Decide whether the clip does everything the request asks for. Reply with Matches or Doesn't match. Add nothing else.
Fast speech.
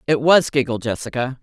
Doesn't match